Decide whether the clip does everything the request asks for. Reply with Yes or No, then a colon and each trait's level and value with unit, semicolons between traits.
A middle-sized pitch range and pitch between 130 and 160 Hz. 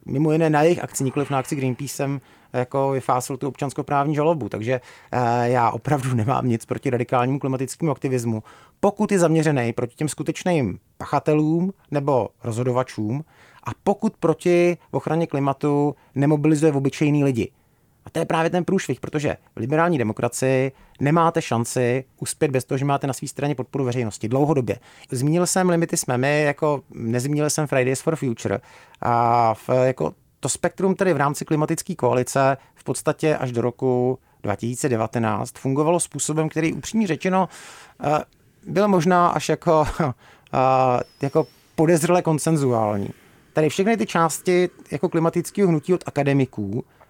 Yes: average, 4.2 semitones; medium, 140 Hz